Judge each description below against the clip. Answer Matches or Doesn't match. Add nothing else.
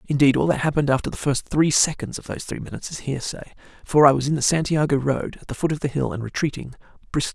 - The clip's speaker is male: Matches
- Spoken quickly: Matches